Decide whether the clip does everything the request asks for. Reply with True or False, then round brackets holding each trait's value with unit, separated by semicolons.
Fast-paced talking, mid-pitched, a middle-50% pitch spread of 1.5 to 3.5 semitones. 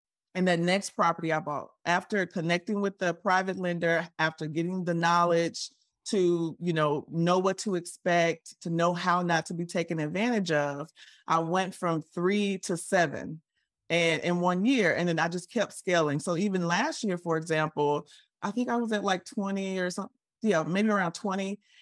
False (185 wpm; 175 Hz; 2.6 semitones)